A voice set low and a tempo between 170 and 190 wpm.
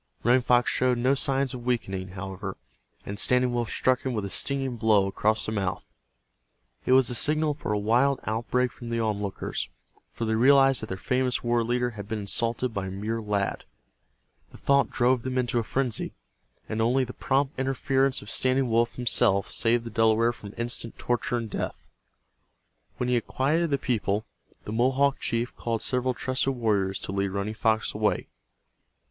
Yes: low, 120 Hz; average, 180 wpm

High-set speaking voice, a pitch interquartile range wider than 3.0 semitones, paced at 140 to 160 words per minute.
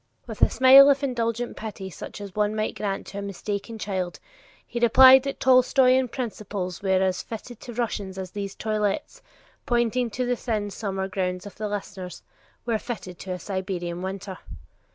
No: high, 210 Hz; average, 4.0 semitones; average, 175 wpm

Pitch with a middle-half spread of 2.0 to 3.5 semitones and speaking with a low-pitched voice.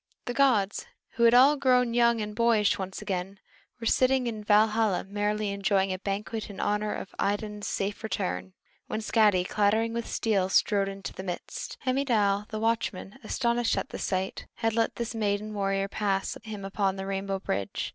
No: narrow, 2.6 semitones; high, 210 Hz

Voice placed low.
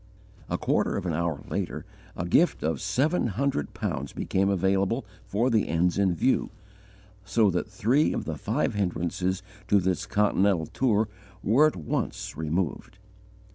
Yes: very low, 95 Hz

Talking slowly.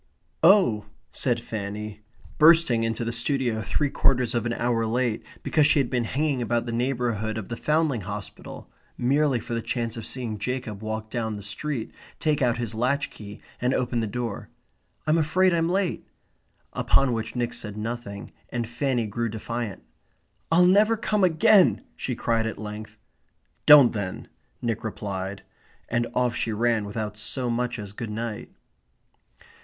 No: average, 160 wpm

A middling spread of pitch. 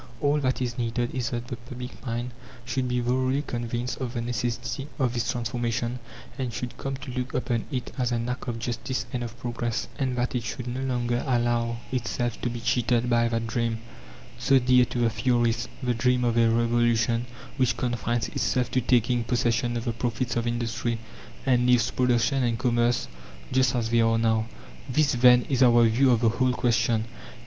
No: narrow, 1.2 semitones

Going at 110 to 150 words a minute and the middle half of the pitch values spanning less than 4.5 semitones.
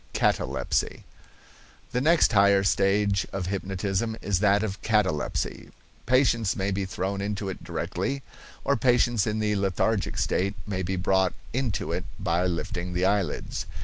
Yes: average, 145 wpm; narrow, 2.4 semitones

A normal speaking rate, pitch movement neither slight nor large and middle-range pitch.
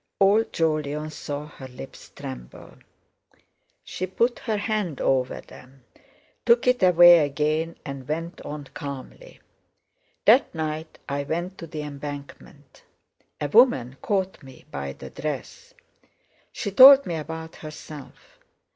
No: slow, 125 wpm; average, 5.0 semitones; medium, 155 Hz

